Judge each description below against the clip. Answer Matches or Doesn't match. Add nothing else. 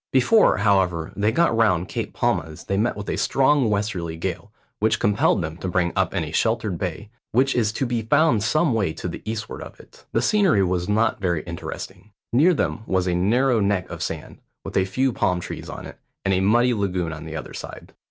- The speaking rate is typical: Doesn't match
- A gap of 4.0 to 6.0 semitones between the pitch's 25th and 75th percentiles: Matches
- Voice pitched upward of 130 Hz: Doesn't match